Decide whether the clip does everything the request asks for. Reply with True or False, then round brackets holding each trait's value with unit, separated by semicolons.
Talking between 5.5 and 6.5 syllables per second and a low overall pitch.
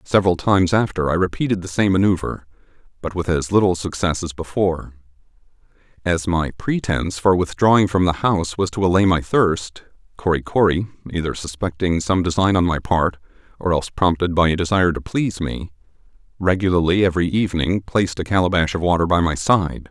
True (5.9 syllables/s; 90 Hz)